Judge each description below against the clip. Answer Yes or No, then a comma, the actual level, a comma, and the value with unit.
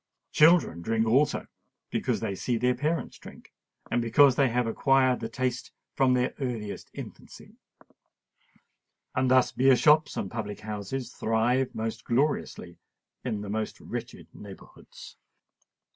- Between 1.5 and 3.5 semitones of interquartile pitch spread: Yes, average, 3.1 semitones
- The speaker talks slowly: Yes, slow, 130 wpm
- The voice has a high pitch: No, low, 125 Hz